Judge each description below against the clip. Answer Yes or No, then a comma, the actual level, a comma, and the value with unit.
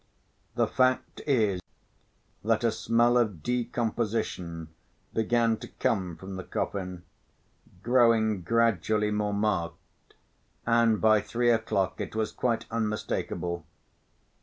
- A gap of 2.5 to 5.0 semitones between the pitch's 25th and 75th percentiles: Yes, average, 3.1 semitones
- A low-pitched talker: Yes, low, 110 Hz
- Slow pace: Yes, slow, 110 wpm